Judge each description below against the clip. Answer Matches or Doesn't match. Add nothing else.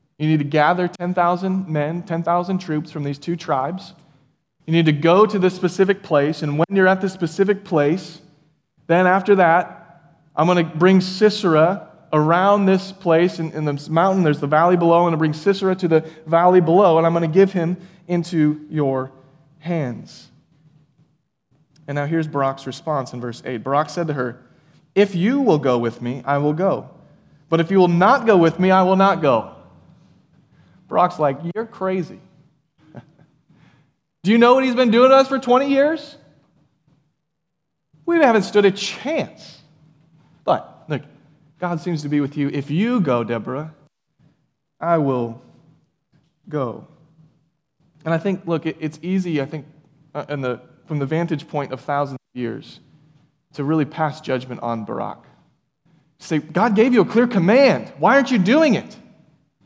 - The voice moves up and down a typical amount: Matches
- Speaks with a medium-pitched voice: Matches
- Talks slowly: Doesn't match